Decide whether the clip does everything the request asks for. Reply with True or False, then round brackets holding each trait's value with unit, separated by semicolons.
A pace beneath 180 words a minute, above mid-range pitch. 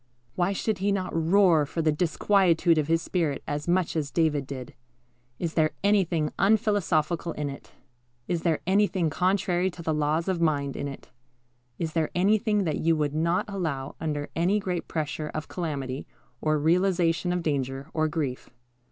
False (170 wpm; 165 Hz)